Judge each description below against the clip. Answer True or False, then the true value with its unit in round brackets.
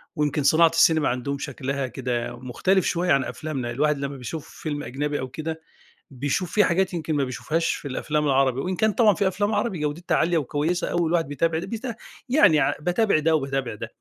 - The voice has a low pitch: False (150 Hz)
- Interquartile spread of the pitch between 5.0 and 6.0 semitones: False (3.9 semitones)